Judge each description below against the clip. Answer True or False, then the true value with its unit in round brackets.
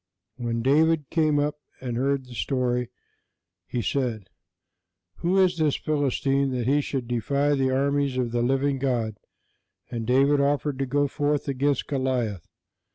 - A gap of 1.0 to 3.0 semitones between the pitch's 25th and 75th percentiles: True (2.7 semitones)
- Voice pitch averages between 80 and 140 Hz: True (135 Hz)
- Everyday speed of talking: True (150 wpm)